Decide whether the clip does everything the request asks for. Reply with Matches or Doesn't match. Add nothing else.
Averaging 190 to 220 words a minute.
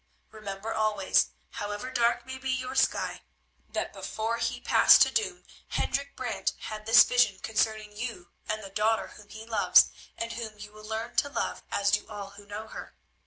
Doesn't match